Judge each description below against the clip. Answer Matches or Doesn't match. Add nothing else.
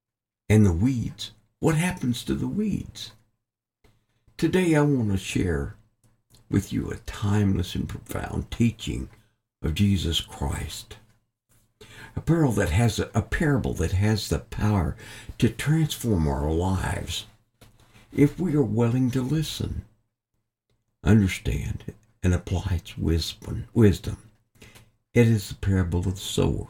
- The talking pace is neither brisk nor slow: Doesn't match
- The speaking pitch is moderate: Doesn't match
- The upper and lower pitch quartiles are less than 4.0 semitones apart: Matches